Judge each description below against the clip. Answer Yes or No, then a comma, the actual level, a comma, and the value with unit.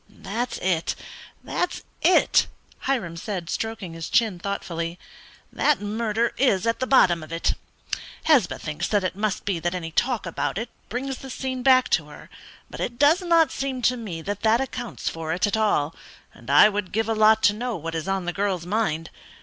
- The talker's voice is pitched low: No, high, 205 Hz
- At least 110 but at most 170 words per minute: No, average, 190 wpm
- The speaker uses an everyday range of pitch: No, wide, 5.9 semitones